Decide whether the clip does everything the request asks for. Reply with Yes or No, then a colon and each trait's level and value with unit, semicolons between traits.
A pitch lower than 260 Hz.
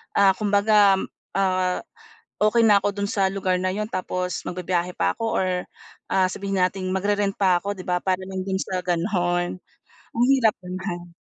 Yes: high, 190 Hz